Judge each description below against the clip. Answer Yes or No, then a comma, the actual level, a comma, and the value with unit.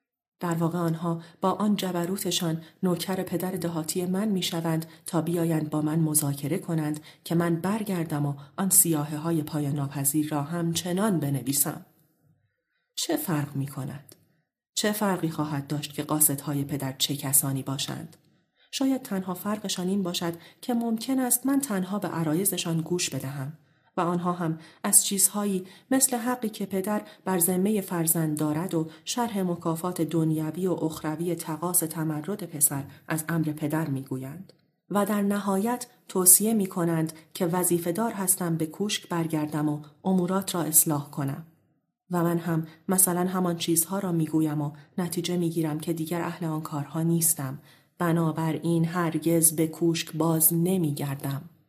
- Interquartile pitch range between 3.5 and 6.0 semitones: No, average, 3.1 semitones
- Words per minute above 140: Yes, average, 150 wpm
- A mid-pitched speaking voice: Yes, medium, 165 Hz